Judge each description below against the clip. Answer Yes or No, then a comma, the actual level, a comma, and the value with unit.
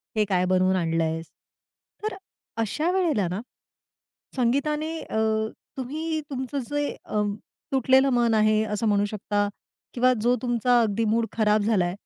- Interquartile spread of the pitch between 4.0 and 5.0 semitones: Yes, average, 4.4 semitones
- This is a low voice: No, high, 225 Hz